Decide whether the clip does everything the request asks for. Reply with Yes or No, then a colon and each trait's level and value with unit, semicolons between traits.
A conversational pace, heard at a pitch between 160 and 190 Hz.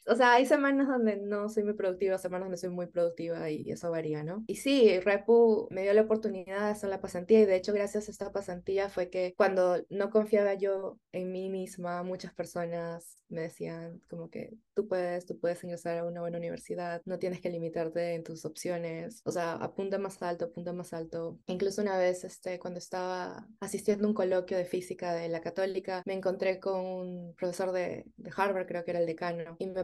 No: fast, 215 wpm; medium, 185 Hz